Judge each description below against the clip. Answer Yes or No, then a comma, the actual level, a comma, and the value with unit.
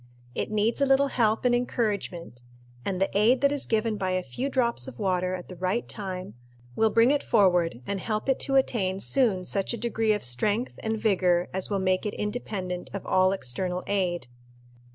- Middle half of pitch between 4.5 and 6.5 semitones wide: No, average, 4.0 semitones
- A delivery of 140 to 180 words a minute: No, average, 195 wpm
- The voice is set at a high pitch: Yes, high, 200 Hz